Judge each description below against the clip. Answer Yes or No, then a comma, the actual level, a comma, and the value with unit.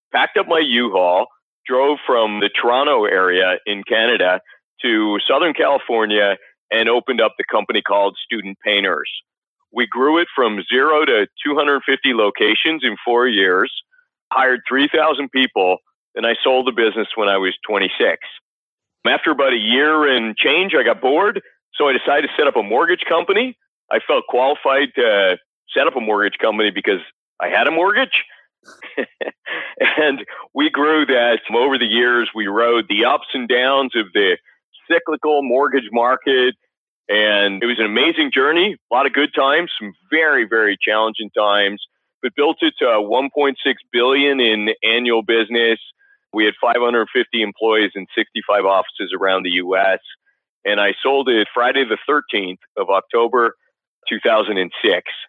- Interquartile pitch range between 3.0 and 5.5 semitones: Yes, average, 4.9 semitones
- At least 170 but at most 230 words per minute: No, average, 155 wpm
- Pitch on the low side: Yes, low, 120 Hz